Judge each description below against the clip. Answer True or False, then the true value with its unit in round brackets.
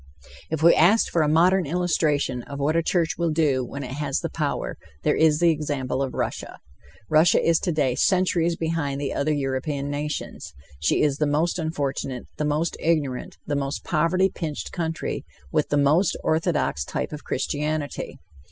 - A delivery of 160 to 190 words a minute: True (170 wpm)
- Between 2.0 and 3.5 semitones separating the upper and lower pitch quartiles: True (2.8 semitones)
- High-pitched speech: False (150 Hz)